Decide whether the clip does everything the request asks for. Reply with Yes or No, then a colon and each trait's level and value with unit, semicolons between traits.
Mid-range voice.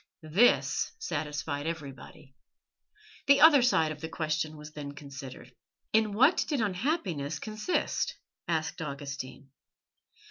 Yes: medium, 155 Hz